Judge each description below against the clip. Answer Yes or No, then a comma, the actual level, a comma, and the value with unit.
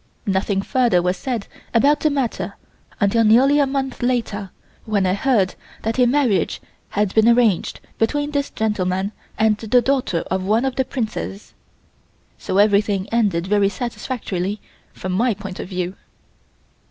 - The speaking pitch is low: No, high, 215 Hz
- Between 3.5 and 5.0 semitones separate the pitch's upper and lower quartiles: Yes, average, 4.4 semitones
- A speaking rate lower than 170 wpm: Yes, average, 150 wpm